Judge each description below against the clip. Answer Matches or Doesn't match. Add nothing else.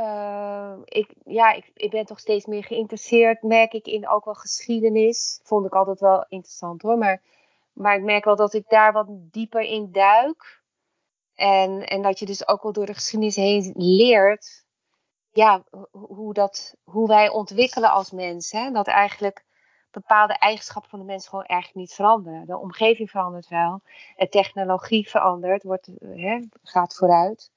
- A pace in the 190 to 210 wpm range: Doesn't match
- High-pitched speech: Matches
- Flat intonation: Matches